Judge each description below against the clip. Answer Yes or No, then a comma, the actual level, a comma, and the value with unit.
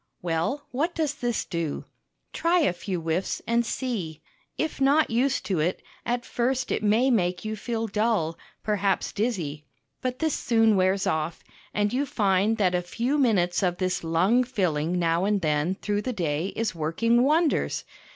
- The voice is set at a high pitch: Yes, high, 205 Hz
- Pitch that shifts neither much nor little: No, wide, 5.7 semitones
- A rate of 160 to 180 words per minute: Yes, average, 170 wpm